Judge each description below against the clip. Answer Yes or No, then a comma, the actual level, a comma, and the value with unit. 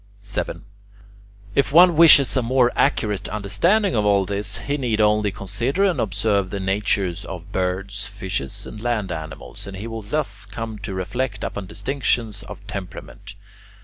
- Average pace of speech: Yes, average, 155 wpm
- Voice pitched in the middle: No, low, 105 Hz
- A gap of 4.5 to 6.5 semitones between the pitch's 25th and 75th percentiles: No, average, 3.6 semitones